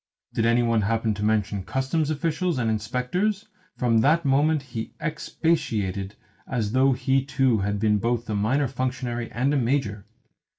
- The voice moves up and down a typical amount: Yes, average, 4.3 semitones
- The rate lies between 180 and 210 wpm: No, average, 160 wpm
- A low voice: Yes, low, 120 Hz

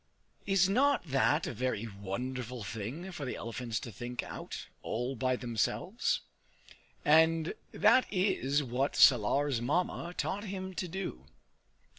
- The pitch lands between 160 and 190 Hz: No, low, 135 Hz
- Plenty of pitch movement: Yes, wide, 7.1 semitones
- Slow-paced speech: Yes, slow, 130 wpm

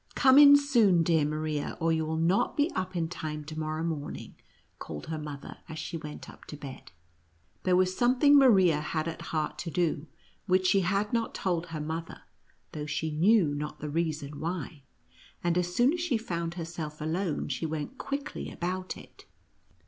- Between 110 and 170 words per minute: No, average, 190 wpm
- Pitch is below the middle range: No, medium, 165 Hz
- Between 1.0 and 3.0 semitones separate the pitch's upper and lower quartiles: No, average, 3.4 semitones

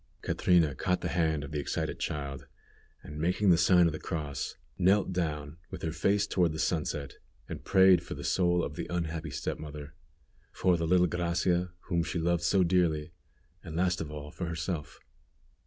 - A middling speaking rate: Yes, average, 180 wpm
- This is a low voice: Yes, very low, 85 Hz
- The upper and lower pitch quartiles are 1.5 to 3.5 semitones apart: Yes, average, 2.8 semitones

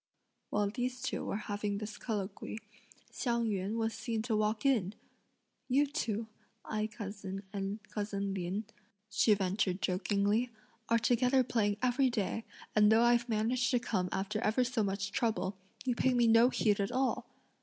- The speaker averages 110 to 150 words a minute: No, average, 165 wpm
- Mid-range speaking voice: No, high, 215 Hz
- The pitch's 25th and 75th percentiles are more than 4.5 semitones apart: No, average, 3.0 semitones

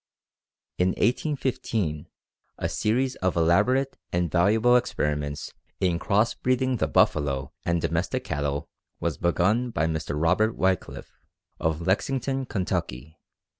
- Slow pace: Yes, slow, 115 wpm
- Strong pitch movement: Yes, wide, 7.1 semitones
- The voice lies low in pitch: Yes, very low, 90 Hz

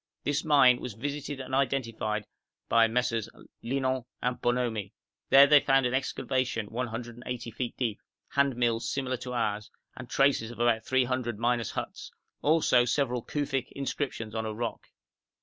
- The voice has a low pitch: Yes, low, 125 Hz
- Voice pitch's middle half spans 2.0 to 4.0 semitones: Yes, narrow, 2.6 semitones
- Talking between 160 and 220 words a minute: No, average, 150 wpm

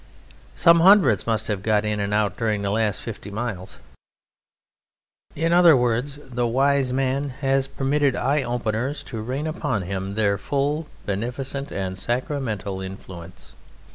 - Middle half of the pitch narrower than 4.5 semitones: No, average, 5.1 semitones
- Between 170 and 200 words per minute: No, average, 140 wpm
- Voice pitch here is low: Yes, low, 120 Hz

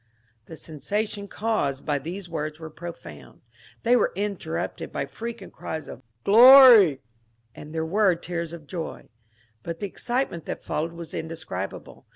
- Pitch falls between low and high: Yes, medium, 170 Hz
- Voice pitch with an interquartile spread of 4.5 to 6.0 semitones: Yes, average, 5.0 semitones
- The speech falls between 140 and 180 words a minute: Yes, average, 160 wpm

